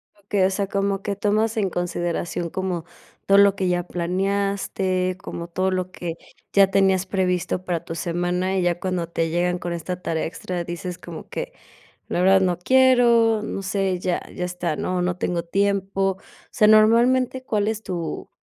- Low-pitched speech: No, medium, 185 Hz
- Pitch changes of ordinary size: No, narrow, 2.1 semitones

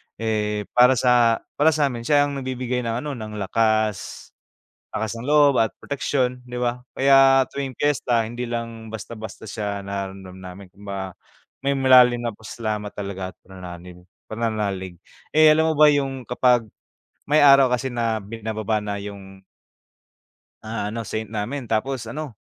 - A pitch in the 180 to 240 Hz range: No, low, 115 Hz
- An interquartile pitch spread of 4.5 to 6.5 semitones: No, average, 3.9 semitones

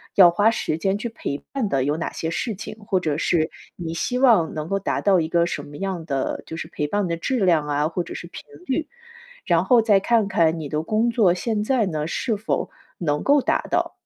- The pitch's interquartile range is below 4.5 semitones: No, average, 5.1 semitones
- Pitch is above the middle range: No, medium, 180 Hz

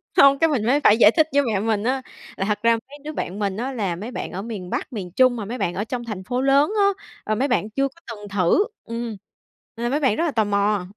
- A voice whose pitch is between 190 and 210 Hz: No, high, 230 Hz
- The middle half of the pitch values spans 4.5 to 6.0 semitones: Yes, average, 4.8 semitones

